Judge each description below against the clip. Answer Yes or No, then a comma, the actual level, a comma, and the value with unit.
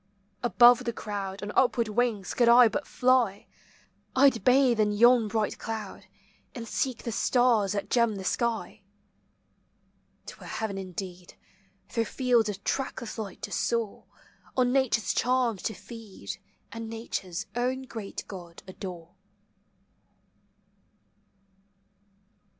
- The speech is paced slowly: Yes, slow, 125 wpm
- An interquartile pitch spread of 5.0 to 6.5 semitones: No, average, 3.4 semitones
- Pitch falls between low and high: No, high, 225 Hz